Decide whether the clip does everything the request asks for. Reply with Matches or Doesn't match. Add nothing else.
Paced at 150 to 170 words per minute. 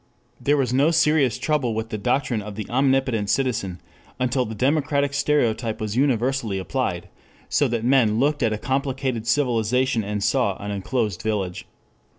Matches